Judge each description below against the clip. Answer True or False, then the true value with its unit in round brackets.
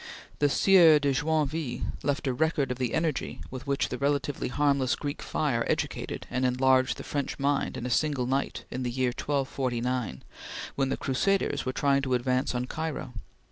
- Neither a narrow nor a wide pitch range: False (2.3 semitones)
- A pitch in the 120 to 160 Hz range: True (135 Hz)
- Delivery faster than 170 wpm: True (180 wpm)